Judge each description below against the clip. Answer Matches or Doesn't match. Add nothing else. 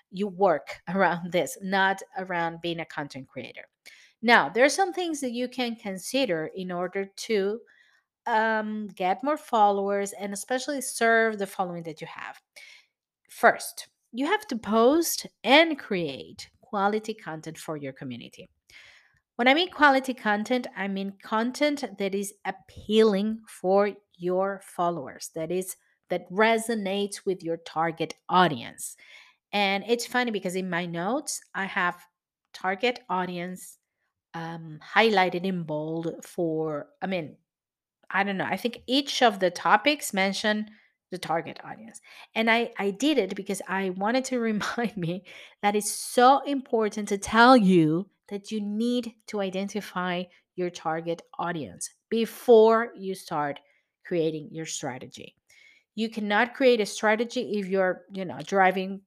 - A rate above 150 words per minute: Doesn't match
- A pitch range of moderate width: Matches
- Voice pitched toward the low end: Doesn't match